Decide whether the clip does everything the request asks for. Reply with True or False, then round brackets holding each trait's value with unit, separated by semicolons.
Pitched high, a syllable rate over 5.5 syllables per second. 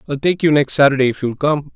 False (140 Hz; 6.5 syllables/s)